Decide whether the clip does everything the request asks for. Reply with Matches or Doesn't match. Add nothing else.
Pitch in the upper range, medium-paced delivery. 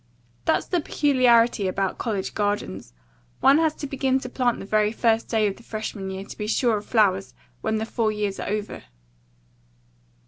Matches